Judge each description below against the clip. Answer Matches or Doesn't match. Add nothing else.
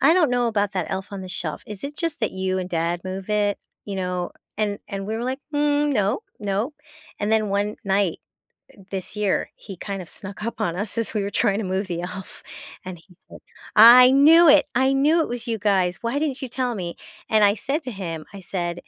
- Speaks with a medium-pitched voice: Doesn't match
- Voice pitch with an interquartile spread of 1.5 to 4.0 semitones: Doesn't match